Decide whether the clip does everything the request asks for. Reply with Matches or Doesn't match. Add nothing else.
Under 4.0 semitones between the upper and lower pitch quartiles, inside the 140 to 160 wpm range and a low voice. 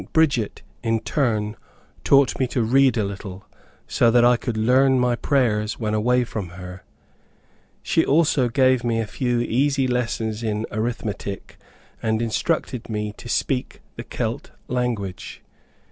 Matches